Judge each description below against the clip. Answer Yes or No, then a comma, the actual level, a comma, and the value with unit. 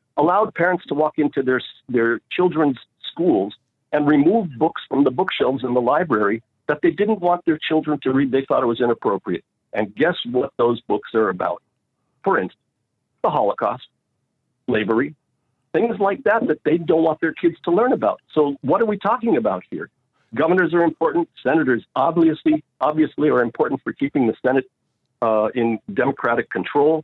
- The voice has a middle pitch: Yes, medium, 155 Hz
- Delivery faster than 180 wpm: No, average, 175 wpm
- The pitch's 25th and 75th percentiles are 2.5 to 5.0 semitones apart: No, wide, 5.6 semitones